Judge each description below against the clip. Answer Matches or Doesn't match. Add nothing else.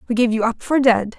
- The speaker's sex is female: Matches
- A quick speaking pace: Matches